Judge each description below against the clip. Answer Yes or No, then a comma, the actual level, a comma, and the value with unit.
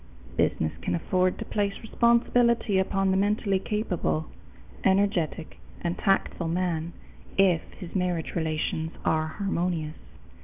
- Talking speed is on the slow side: Yes, slow, 115 wpm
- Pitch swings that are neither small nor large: Yes, average, 3.3 semitones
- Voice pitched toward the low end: No, medium, 185 Hz